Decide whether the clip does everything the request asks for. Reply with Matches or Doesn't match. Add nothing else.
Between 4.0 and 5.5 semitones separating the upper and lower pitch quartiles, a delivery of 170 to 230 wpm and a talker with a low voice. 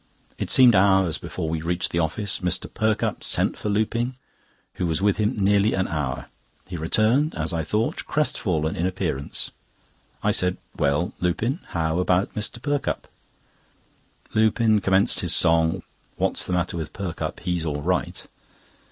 Doesn't match